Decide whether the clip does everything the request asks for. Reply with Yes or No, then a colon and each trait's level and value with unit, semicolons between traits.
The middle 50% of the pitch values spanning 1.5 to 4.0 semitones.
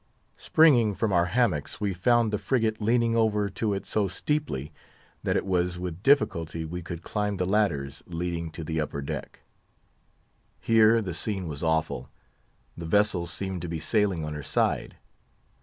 No: average, 4.7 semitones